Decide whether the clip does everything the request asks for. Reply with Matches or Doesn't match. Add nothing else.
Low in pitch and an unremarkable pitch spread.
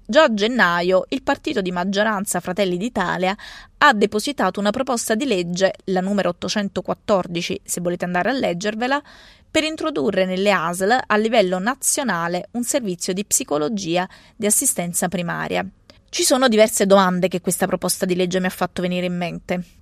Doesn't match